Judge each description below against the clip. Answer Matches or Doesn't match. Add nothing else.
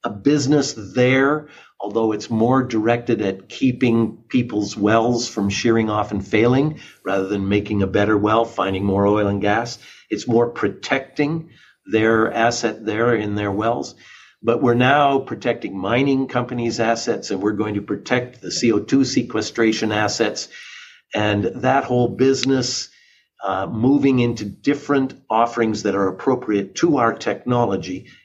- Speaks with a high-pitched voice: Doesn't match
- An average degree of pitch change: Matches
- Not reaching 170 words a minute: Matches